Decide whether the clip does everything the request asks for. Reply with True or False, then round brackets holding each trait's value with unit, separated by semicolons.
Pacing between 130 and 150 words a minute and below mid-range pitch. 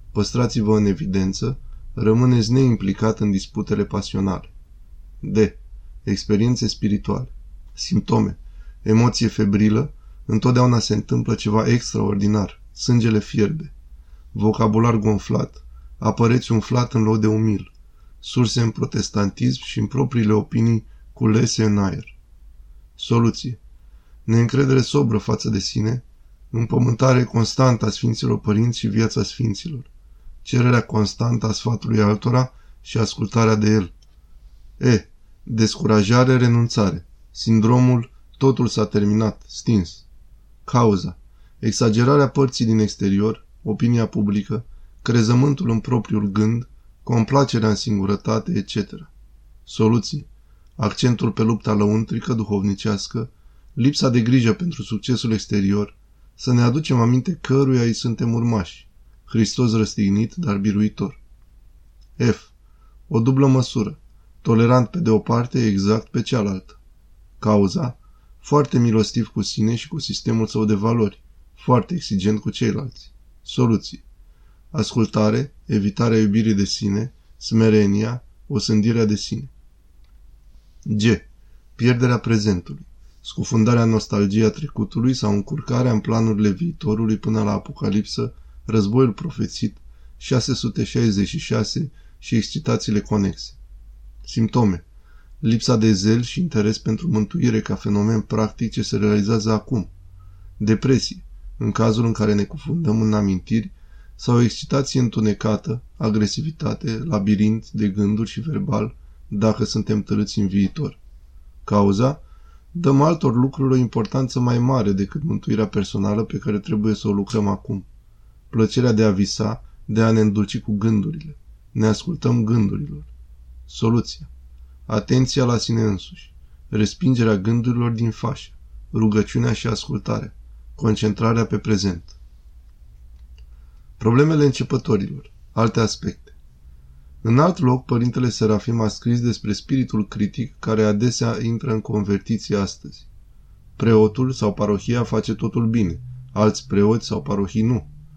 False (115 wpm; 110 Hz)